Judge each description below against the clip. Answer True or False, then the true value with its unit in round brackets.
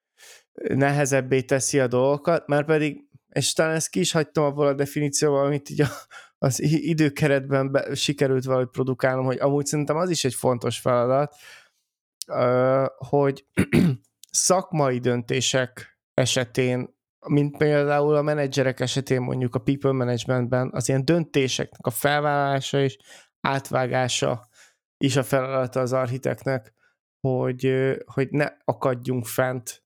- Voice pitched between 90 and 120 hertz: False (135 Hz)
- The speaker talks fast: False (125 wpm)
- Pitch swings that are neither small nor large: False (2.0 semitones)